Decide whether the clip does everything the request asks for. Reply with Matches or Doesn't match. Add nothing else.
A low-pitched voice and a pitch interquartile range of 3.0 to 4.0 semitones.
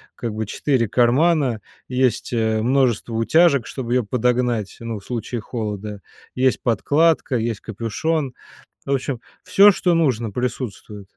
Matches